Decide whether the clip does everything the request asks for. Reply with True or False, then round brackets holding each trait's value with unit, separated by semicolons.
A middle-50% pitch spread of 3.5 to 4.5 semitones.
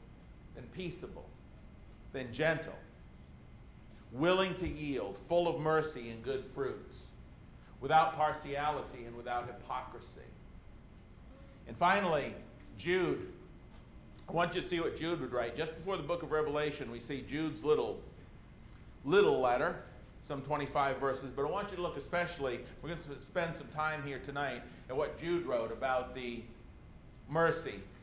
False (5.2 semitones)